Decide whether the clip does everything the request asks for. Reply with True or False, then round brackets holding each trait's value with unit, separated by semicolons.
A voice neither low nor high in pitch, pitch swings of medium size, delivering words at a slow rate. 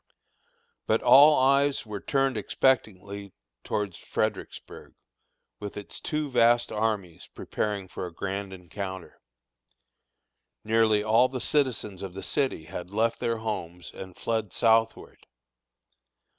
False (110 Hz; 3.7 semitones; 115 wpm)